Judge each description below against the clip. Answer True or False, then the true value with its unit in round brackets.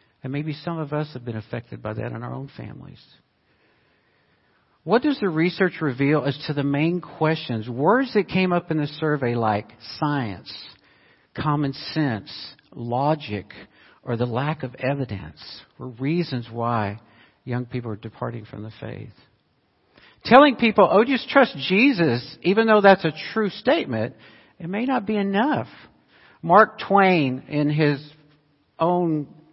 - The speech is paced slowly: False (150 wpm)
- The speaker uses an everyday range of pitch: False (6.7 semitones)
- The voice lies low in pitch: False (150 Hz)